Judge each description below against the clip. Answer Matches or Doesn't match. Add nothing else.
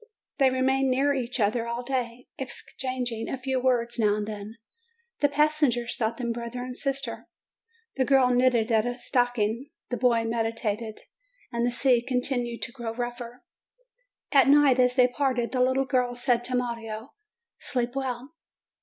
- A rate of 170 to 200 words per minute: Doesn't match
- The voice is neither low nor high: Doesn't match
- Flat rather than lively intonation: Matches